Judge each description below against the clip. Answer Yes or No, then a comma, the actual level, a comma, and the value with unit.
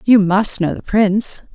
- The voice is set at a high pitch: Yes, high, 205 Hz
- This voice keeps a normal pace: Yes, average, 195 wpm